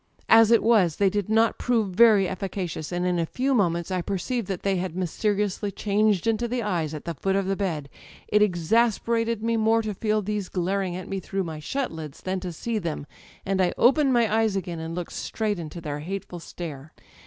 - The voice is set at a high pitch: Yes, high, 195 Hz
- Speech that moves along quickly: Yes, fast, 210 wpm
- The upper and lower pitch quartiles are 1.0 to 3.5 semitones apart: No, average, 3.9 semitones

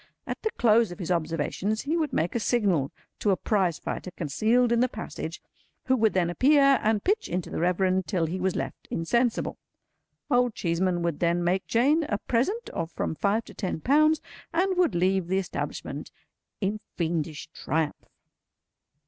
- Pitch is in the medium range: No, high, 195 Hz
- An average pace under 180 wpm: Yes, average, 170 wpm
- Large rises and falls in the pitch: Yes, wide, 6.0 semitones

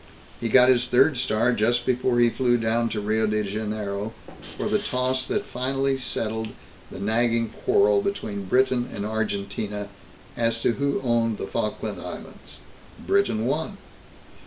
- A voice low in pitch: Yes, low, 120 Hz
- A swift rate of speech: No, average, 150 wpm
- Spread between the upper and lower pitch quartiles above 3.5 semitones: No, average, 3.1 semitones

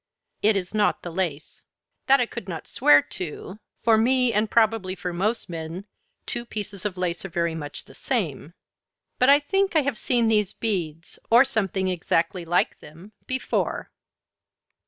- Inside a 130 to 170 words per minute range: Yes, average, 165 wpm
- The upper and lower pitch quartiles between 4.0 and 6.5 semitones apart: Yes, average, 5.0 semitones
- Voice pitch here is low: No, high, 195 Hz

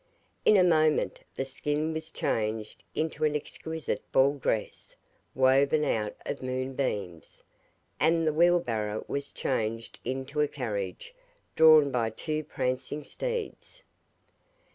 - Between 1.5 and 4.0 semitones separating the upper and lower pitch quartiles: No, average, 4.8 semitones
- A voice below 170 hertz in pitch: Yes, medium, 140 Hz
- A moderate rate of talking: No, slow, 125 wpm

